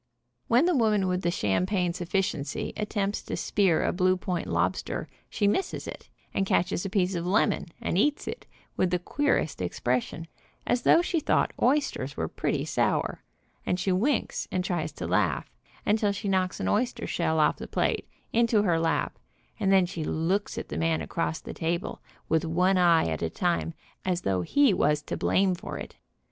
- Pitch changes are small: No, average, 3.8 semitones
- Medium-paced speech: Yes, average, 185 wpm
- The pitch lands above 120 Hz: Yes, medium, 185 Hz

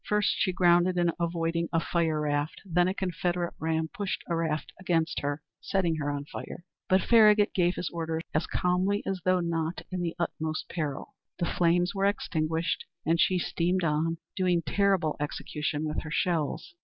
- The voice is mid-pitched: Yes, medium, 170 Hz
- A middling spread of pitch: No, narrow, 2.3 semitones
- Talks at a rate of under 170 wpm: No, average, 175 wpm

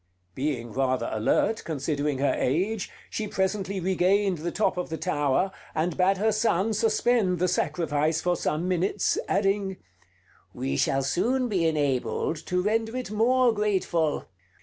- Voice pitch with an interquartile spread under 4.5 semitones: No, average, 5.3 semitones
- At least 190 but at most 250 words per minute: No, average, 145 wpm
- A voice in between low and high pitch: Yes, medium, 180 Hz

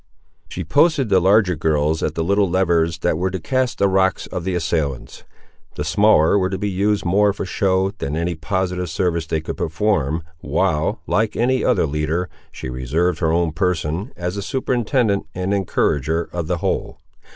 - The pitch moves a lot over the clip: No, average, 3.8 semitones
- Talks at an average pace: Yes, average, 180 wpm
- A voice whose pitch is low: Yes, very low, 90 Hz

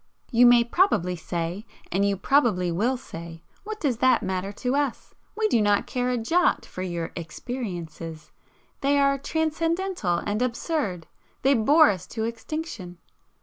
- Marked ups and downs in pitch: Yes, wide, 7.6 semitones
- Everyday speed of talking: Yes, average, 150 wpm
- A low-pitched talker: No, high, 230 Hz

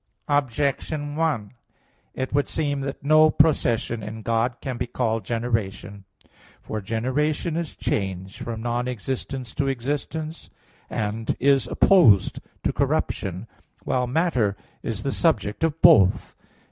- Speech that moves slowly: Yes, slow, 125 wpm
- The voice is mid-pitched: No, low, 125 Hz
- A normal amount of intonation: Yes, average, 4.8 semitones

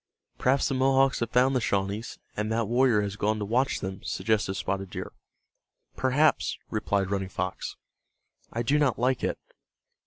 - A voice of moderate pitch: No, low, 115 Hz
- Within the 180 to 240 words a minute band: No, average, 160 wpm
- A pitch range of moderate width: Yes, average, 4.5 semitones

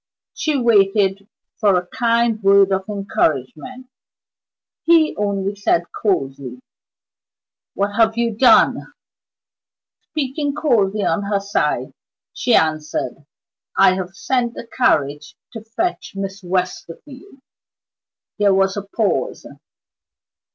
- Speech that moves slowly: Yes, slow, 105 wpm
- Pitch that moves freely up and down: No, average, 3.7 semitones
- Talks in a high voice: Yes, high, 200 Hz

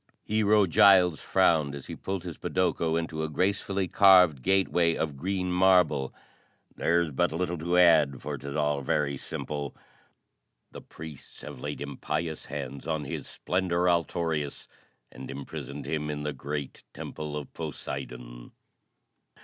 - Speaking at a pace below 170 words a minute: Yes, average, 140 wpm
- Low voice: Yes, very low, 80 Hz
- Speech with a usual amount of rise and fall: Yes, average, 3.9 semitones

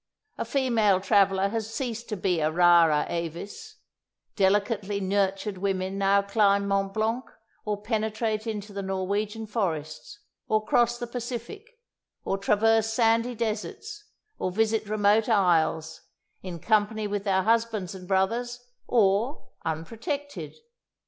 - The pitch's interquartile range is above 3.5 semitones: No, average, 2.9 semitones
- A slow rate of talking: Yes, slow, 125 wpm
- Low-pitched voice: No, high, 210 Hz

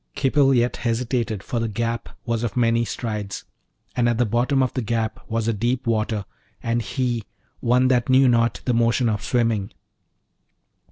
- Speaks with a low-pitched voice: Yes, low, 115 Hz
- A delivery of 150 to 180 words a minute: Yes, average, 170 wpm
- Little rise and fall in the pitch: Yes, narrow, 1.6 semitones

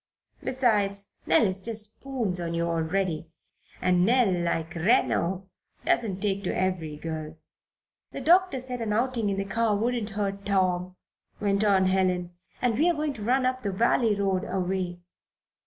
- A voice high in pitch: Yes, high, 200 Hz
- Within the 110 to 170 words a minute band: Yes, average, 160 wpm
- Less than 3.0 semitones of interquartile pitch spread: No, average, 4.1 semitones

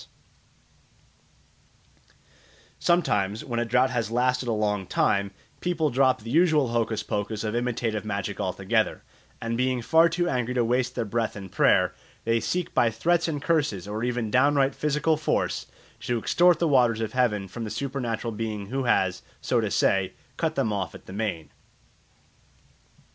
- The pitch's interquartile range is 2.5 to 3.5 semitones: No, average, 4.2 semitones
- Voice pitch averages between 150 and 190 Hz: No, low, 120 Hz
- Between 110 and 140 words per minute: No, average, 160 wpm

